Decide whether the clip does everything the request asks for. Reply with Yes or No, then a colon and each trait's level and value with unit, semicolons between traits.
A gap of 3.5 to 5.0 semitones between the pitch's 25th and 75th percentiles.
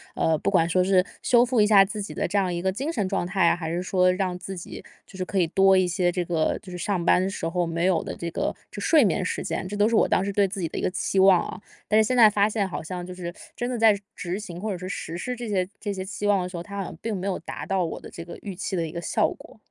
No: narrow, 2.5 semitones